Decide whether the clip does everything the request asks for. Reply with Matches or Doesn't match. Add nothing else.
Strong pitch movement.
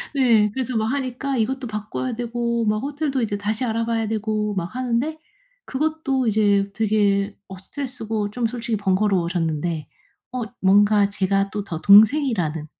Doesn't match